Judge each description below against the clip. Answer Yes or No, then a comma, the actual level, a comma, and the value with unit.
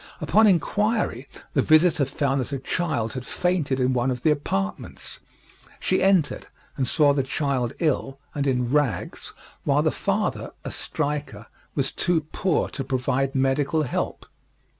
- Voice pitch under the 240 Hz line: Yes, medium, 140 Hz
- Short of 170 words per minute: Yes, average, 150 wpm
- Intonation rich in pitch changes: No, average, 3.4 semitones